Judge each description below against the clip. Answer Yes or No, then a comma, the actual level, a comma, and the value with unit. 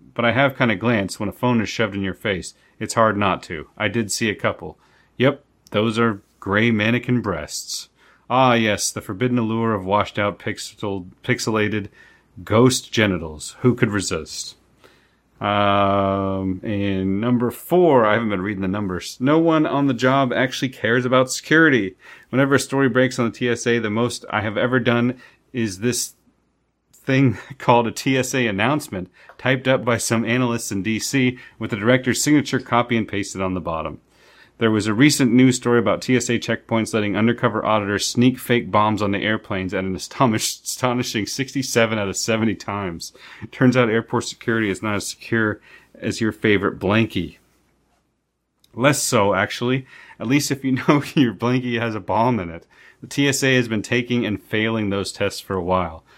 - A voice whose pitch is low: Yes, low, 115 Hz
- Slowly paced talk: No, average, 175 wpm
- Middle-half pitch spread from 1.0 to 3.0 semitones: No, average, 3.7 semitones